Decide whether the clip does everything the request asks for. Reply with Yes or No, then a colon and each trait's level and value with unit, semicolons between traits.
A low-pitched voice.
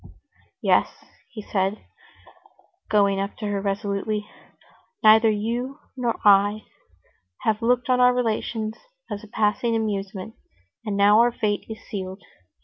No: high, 215 Hz